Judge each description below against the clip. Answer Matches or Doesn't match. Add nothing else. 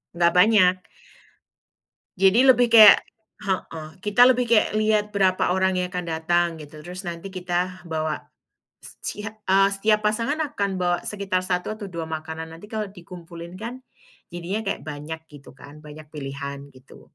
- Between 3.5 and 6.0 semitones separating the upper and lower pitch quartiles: Matches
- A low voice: Doesn't match